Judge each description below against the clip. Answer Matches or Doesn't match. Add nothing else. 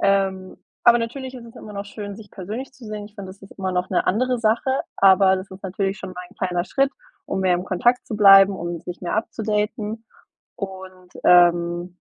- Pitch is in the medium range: Doesn't match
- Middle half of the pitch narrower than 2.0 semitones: Doesn't match